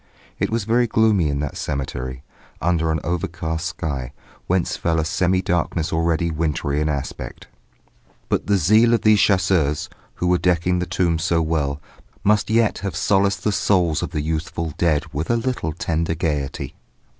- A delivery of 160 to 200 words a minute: Yes, average, 170 wpm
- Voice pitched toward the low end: Yes, very low, 85 Hz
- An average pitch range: Yes, average, 3.6 semitones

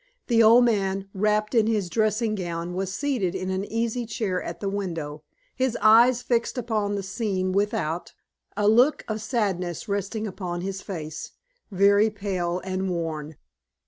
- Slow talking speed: No, average, 155 wpm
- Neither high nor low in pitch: No, high, 200 Hz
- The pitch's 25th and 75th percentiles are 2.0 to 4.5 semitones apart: Yes, average, 3.2 semitones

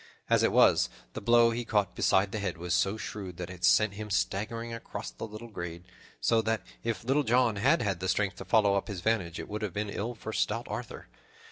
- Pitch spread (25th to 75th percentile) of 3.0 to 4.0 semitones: Yes, average, 3.3 semitones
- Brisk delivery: Yes, fast, 230 wpm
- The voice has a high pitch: No, low, 105 Hz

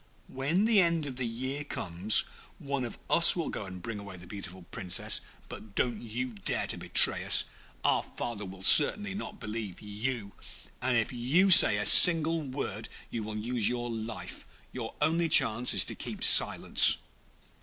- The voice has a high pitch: No, low, 120 Hz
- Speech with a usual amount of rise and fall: No, wide, 6.1 semitones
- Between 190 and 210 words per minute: No, average, 170 wpm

